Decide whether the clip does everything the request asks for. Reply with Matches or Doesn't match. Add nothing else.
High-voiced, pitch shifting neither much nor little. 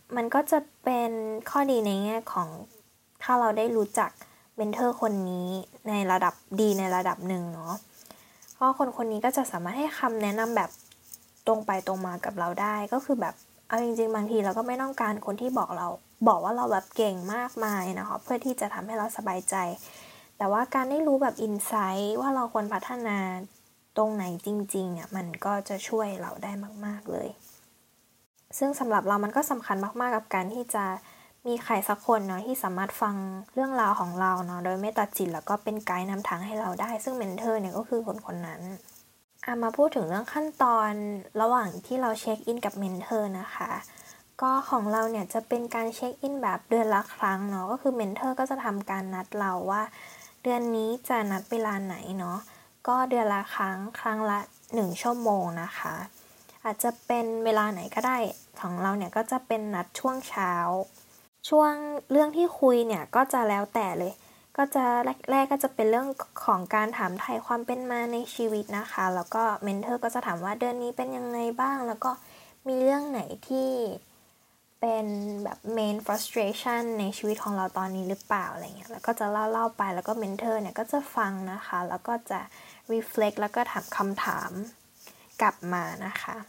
Matches